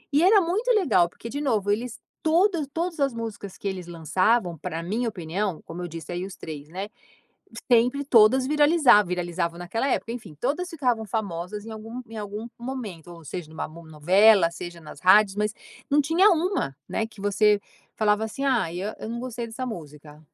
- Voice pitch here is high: Yes, high, 215 Hz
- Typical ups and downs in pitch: No, wide, 6.5 semitones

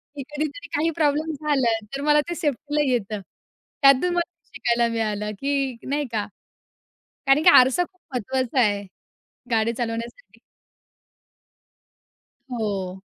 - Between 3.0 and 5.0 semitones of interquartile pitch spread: Yes, average, 4.7 semitones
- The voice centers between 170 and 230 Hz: No, very high, 265 Hz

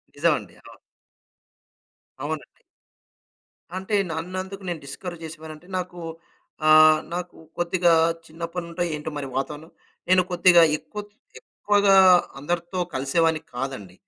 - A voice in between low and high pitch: Yes, medium, 170 Hz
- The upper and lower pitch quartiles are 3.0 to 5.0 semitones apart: No, narrow, 2.6 semitones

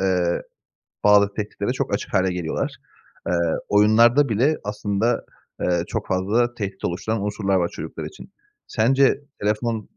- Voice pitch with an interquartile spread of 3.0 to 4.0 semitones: Yes, average, 3.3 semitones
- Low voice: Yes, low, 105 Hz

